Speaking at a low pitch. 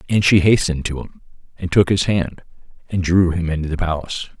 Yes: very low, 90 Hz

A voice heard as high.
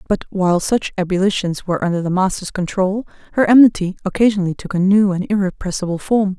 Yes: high, 195 Hz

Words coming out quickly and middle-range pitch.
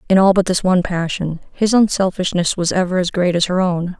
Yes: fast, 225 wpm; medium, 180 Hz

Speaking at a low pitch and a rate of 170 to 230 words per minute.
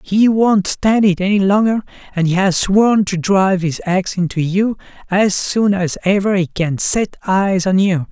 No: high, 190 Hz; average, 185 wpm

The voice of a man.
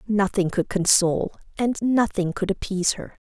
No: female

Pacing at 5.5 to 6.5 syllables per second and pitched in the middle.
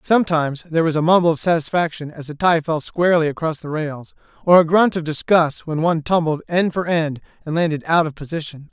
Yes: 6.0 syllables/s; medium, 160 Hz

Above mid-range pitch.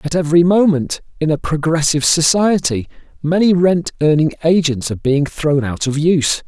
No: medium, 155 Hz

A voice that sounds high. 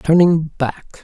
No: medium, 160 Hz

